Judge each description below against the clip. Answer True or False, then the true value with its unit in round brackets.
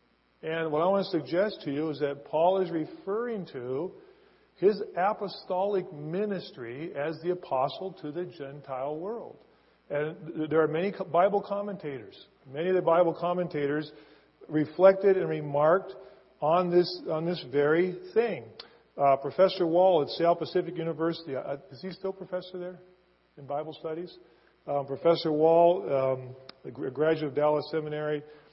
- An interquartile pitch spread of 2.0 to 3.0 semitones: False (3.7 semitones)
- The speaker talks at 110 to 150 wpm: True (145 wpm)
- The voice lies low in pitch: False (165 Hz)